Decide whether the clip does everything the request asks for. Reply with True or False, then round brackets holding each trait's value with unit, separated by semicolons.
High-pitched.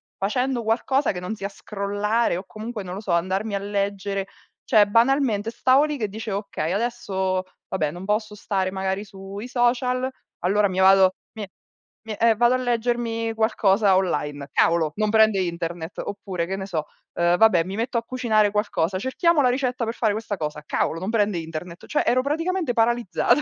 True (205 Hz)